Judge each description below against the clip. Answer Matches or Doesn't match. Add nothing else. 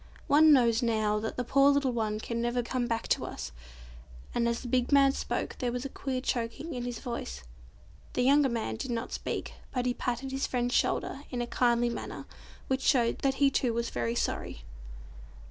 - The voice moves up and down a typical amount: Doesn't match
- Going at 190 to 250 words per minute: Matches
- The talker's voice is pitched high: Matches